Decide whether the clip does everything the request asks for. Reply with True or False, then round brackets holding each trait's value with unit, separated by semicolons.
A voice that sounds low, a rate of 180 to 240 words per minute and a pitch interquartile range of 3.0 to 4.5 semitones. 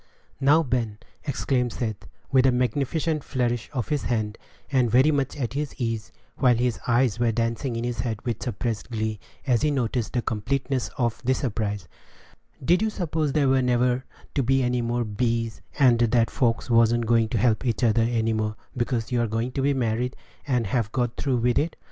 False (120 Hz; 195 wpm; 2.5 semitones)